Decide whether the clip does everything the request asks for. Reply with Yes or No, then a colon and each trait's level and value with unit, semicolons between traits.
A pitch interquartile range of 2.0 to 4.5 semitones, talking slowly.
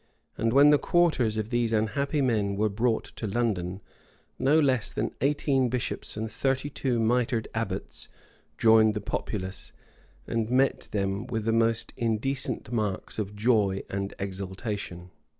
No: average, 3.4 semitones; average, 145 wpm